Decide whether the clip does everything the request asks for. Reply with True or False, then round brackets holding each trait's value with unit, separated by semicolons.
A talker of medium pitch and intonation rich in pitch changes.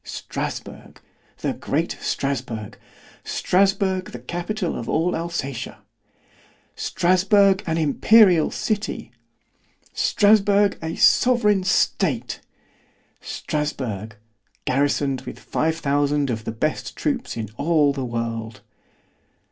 True (160 Hz; 6.6 semitones)